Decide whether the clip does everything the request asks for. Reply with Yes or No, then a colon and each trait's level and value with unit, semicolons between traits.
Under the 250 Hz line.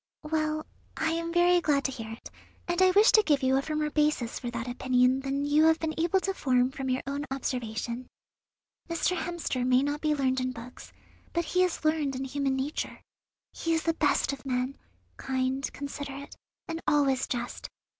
No: very high, 280 Hz